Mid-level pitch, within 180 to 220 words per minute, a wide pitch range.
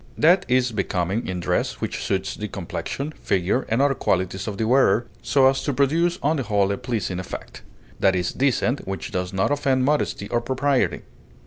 No: low, 120 Hz; average, 190 wpm; wide, 6.1 semitones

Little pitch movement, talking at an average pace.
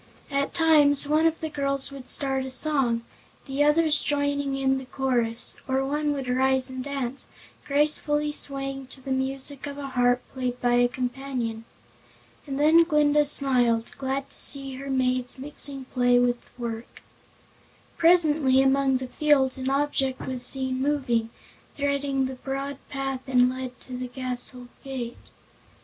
Yes: narrow, 1.9 semitones; average, 155 wpm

